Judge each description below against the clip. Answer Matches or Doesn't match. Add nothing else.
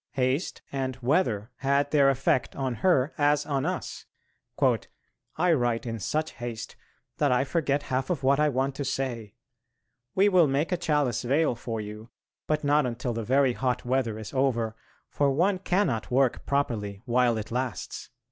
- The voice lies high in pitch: Doesn't match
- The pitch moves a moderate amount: Matches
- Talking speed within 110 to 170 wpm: Matches